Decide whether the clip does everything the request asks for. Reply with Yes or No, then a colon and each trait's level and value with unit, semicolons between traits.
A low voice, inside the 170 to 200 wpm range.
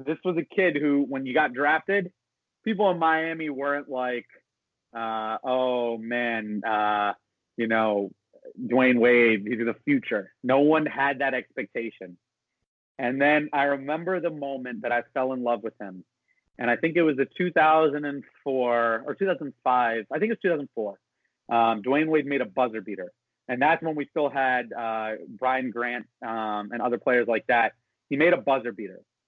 No: low, 130 Hz; average, 160 wpm